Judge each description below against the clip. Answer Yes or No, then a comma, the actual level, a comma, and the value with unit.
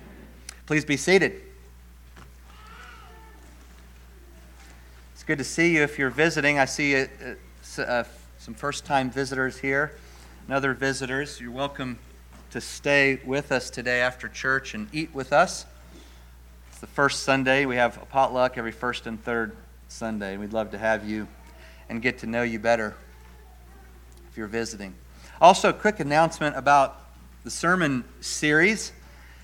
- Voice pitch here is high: No, low, 115 Hz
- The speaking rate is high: No, average, 145 wpm